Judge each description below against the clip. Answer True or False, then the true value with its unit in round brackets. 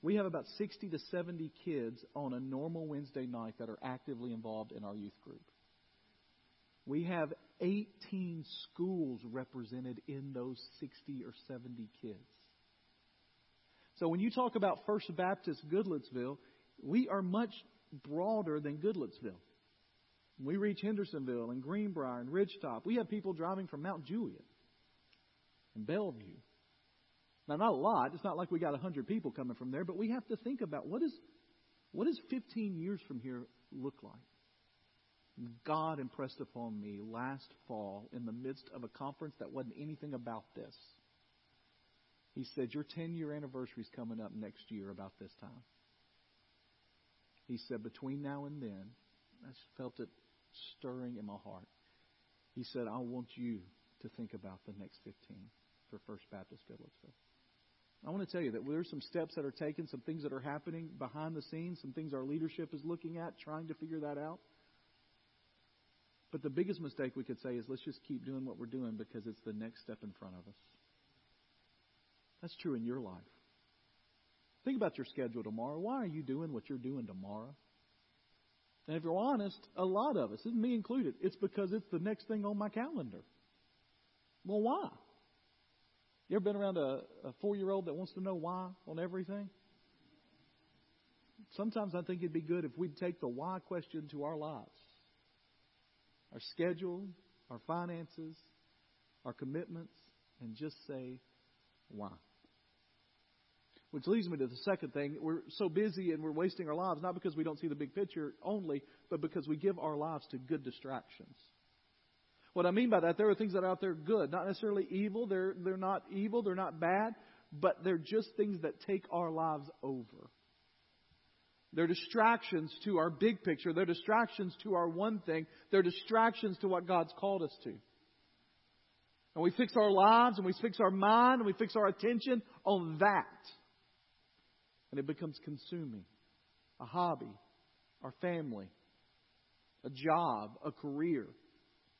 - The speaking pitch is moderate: True (155 Hz)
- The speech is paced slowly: False (170 wpm)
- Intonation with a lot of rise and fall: True (8.0 semitones)